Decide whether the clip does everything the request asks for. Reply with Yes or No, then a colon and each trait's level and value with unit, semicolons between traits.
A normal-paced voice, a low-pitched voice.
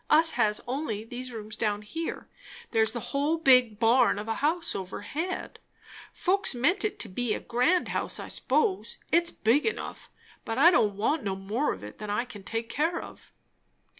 No: average, 185 wpm; high, 245 Hz